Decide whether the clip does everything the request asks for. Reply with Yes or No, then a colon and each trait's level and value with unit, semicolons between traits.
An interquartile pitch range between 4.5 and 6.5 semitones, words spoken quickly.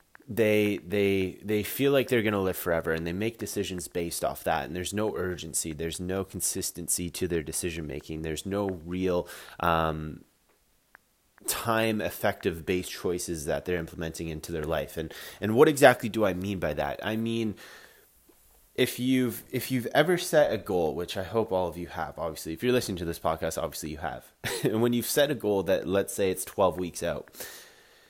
Yes: average, 4.8 semitones; fast, 210 wpm